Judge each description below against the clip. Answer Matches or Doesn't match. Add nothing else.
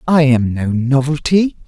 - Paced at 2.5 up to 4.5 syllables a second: Matches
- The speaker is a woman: Doesn't match